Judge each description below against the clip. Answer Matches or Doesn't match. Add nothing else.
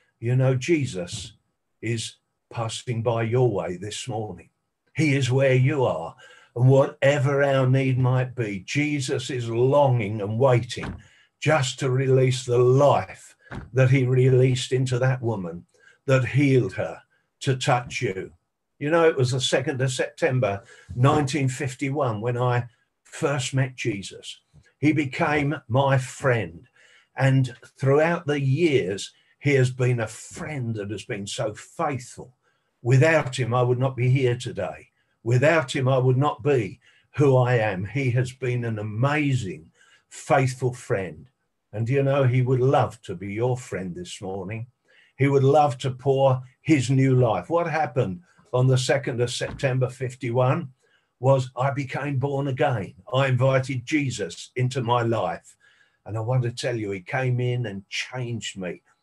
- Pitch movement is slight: Matches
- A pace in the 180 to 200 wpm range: Doesn't match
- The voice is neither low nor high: Doesn't match